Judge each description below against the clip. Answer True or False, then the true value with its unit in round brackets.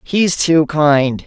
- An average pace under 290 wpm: True (140 wpm)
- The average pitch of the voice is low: False (155 Hz)